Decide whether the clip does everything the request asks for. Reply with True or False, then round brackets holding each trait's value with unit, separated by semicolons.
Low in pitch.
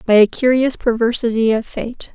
False (235 Hz)